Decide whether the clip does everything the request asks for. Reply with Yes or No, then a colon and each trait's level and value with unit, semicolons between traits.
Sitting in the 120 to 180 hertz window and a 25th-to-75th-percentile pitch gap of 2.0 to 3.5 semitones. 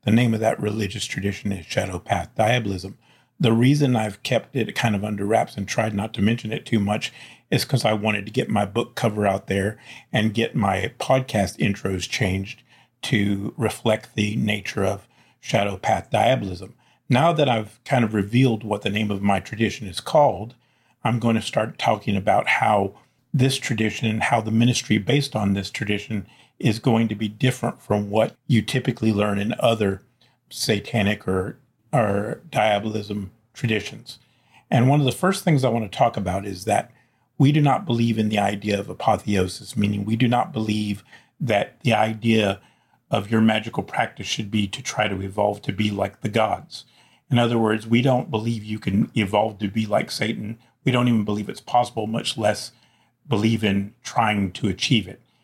No: low, 110 Hz; average, 2.8 semitones